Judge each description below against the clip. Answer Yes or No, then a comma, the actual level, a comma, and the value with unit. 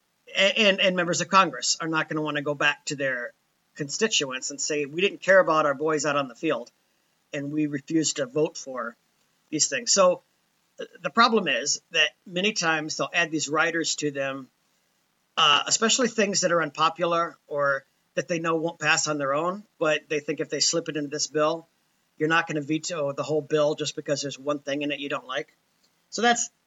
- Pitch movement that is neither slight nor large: Yes, average, 3.0 semitones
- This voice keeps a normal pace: No, fast, 215 wpm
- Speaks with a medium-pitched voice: Yes, medium, 155 Hz